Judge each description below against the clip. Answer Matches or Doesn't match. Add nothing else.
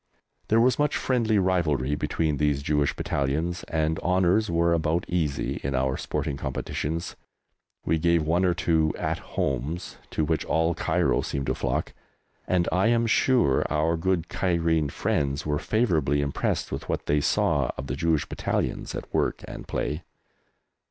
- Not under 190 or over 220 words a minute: Doesn't match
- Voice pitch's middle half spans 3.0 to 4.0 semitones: Matches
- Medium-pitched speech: Doesn't match